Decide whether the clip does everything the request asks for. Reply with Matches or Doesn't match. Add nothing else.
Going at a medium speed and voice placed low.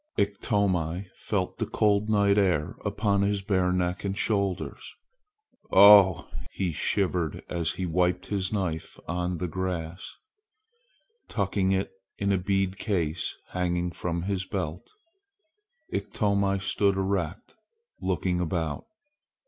Doesn't match